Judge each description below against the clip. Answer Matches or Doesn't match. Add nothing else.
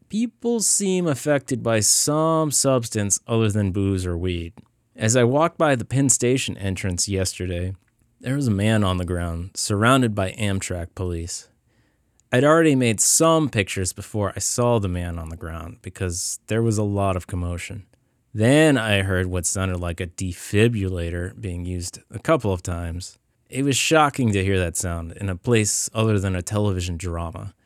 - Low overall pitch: Matches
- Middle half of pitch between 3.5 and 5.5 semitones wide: Matches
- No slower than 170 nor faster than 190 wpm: Matches